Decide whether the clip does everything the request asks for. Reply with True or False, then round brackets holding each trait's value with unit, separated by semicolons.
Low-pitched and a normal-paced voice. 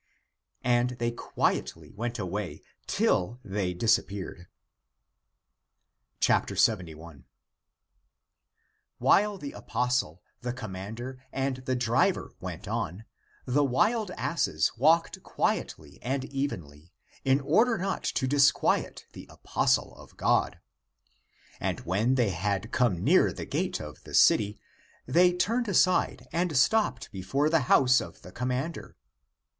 False (125 Hz; 115 wpm)